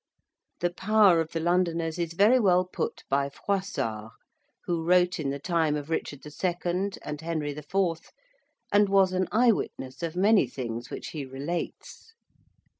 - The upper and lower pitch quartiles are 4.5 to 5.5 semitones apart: No, average, 4.0 semitones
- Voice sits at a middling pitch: Yes, medium, 170 Hz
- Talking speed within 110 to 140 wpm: No, average, 150 wpm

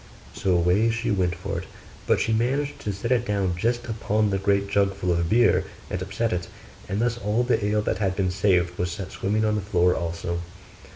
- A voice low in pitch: Yes, low, 100 Hz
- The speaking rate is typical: No, fast, 220 wpm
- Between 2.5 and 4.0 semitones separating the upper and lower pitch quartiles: Yes, average, 3.6 semitones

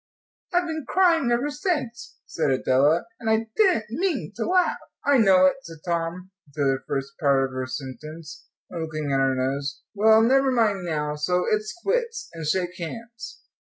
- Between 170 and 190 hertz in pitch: Yes, medium, 185 Hz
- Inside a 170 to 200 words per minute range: Yes, average, 175 wpm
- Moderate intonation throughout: No, wide, 9.0 semitones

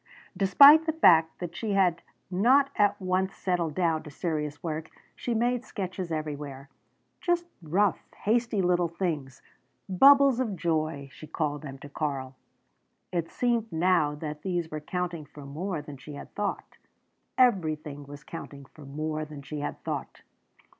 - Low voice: No, medium, 165 Hz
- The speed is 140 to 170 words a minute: Yes, average, 155 wpm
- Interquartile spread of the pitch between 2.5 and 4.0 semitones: No, average, 4.7 semitones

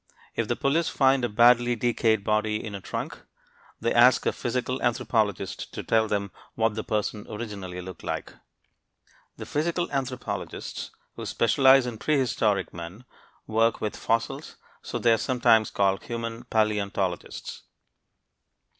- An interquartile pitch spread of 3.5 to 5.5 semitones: No, average, 2.8 semitones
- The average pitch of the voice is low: Yes, low, 115 Hz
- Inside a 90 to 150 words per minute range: Yes, slow, 135 wpm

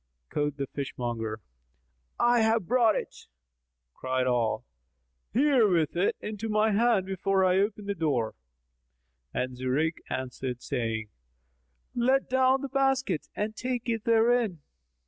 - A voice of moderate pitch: No, high, 195 Hz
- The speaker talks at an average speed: No, slow, 125 wpm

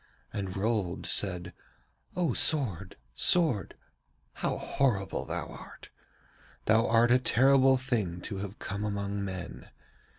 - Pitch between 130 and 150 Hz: No, low, 105 Hz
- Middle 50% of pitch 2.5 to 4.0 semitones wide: No, average, 4.8 semitones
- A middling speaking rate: No, slow, 120 wpm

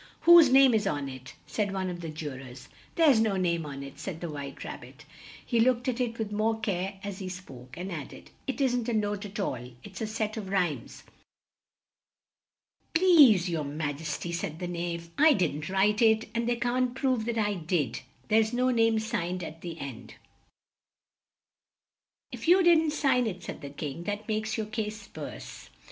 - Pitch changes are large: Yes, wide, 5.7 semitones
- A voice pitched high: Yes, high, 205 Hz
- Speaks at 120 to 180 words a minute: No, average, 195 wpm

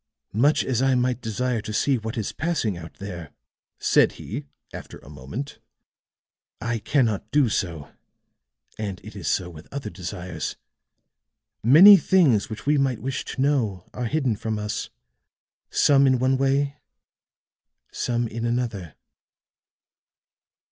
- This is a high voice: No, low, 120 Hz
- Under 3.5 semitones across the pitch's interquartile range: No, average, 4.8 semitones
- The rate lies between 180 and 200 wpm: No, slow, 135 wpm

